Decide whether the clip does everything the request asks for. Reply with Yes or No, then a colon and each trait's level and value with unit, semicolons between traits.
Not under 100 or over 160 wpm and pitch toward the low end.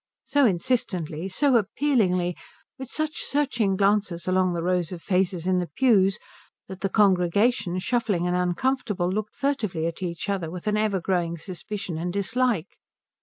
No: average, 155 wpm; high, 190 Hz